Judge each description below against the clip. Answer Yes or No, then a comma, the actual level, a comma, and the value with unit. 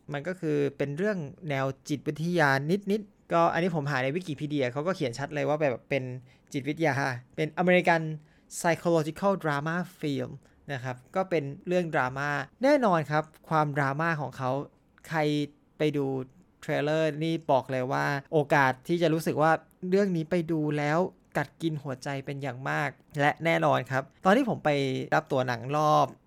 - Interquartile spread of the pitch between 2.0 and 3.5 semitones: Yes, average, 3.0 semitones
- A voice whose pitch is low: No, medium, 150 Hz